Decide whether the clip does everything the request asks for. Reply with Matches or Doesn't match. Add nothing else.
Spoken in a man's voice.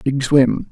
Matches